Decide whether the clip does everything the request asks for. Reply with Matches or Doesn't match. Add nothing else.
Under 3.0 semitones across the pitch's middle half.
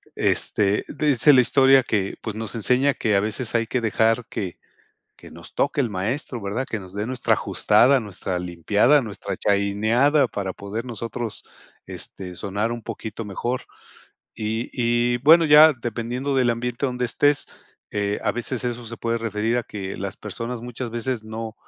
Doesn't match